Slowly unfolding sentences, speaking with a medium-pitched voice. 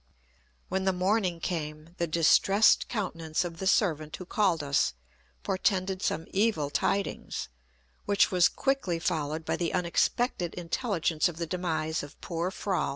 No: average, 145 wpm; medium, 175 Hz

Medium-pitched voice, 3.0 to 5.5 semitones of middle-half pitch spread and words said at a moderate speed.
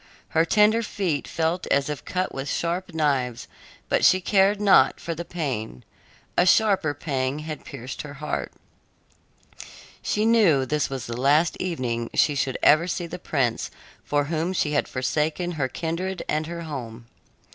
Yes: medium, 155 Hz; average, 4.6 semitones; average, 160 wpm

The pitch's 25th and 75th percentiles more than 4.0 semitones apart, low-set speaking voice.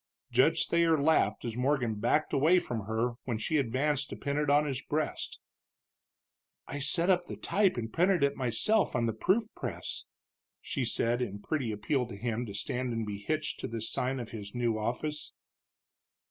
Yes: average, 4.9 semitones; low, 125 Hz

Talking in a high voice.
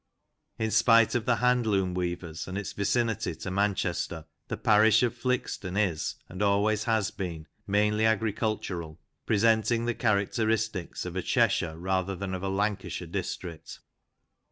No: low, 105 Hz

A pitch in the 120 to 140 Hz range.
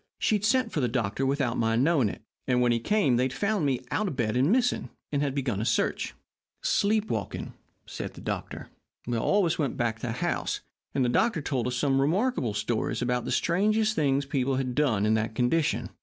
Yes: low, 135 Hz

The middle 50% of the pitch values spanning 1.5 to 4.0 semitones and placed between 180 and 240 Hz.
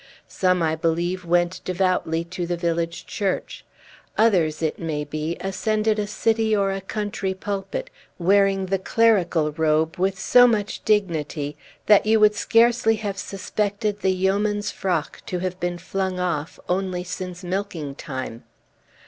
Yes: average, 3.4 semitones; medium, 185 Hz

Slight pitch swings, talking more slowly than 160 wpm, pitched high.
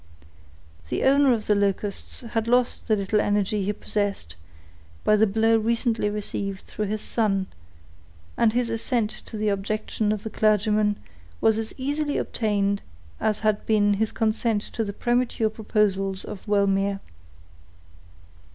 Yes: narrow, 1.8 semitones; average, 140 wpm; high, 215 Hz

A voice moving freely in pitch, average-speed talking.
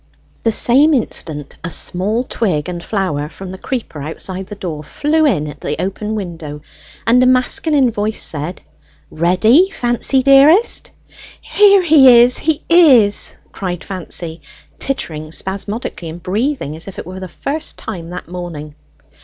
Yes: wide, 7.2 semitones; average, 150 wpm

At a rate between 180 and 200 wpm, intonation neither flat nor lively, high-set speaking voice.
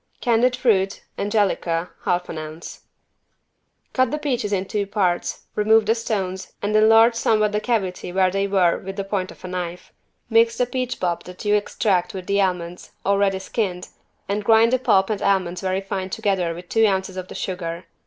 Yes: average, 185 wpm; average, 3.0 semitones; high, 195 Hz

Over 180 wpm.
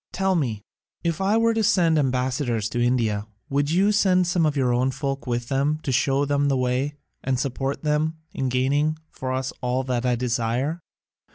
Yes: average, 190 wpm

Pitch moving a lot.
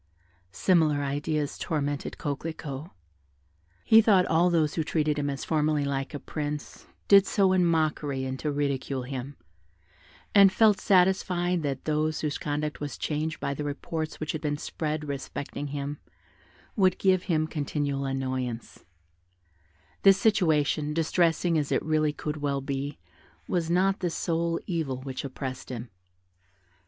No: average, 3.0 semitones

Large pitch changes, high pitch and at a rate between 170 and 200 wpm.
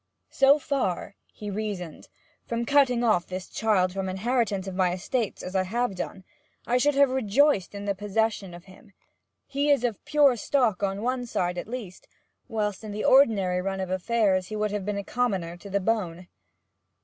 No: average, 4.5 semitones; high, 210 Hz; average, 185 wpm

